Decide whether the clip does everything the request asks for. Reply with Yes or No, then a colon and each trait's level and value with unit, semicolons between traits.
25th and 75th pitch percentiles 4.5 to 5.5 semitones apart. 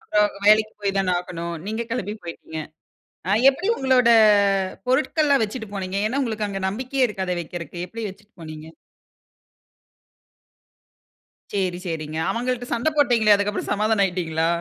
Yes: average, 4.9 semitones